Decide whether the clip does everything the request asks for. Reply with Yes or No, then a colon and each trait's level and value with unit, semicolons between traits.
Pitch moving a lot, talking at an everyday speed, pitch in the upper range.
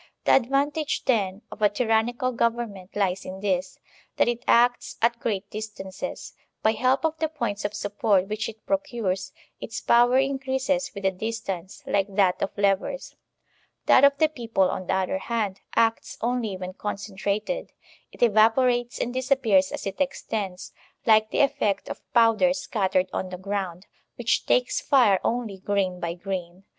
No: average, 4.2 semitones; average, 160 wpm; high, 215 Hz